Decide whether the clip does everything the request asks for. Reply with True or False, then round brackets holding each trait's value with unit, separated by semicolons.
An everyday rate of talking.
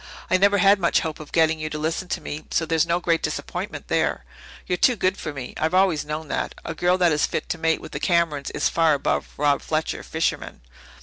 False (235 wpm)